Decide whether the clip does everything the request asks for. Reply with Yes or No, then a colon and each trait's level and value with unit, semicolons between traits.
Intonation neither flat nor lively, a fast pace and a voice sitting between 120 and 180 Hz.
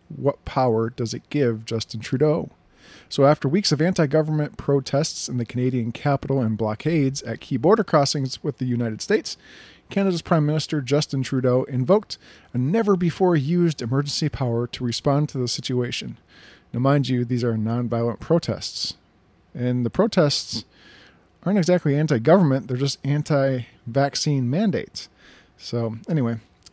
No: average, 4.3 semitones; average, 150 wpm; low, 135 Hz